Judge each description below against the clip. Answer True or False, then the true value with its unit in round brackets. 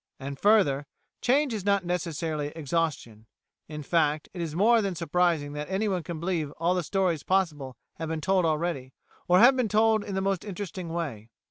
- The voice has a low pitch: False (170 Hz)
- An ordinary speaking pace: True (185 wpm)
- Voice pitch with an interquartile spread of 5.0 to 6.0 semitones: False (4.3 semitones)